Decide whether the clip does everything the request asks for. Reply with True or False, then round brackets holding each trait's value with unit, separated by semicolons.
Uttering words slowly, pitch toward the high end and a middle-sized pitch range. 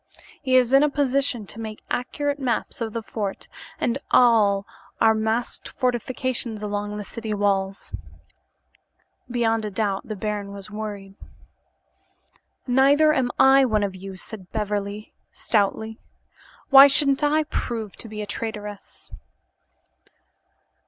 True (130 wpm; 220 Hz; 3.9 semitones)